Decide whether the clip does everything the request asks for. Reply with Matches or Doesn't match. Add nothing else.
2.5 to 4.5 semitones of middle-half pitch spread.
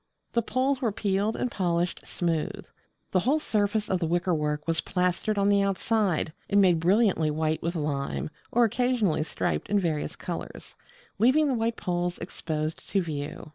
Doesn't match